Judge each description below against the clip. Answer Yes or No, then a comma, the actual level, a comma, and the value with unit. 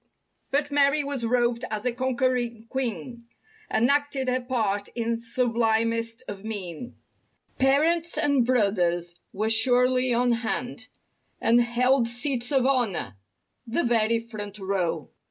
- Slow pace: Yes, slow, 120 wpm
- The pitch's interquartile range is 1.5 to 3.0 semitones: Yes, average, 2.7 semitones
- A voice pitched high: Yes, high, 235 Hz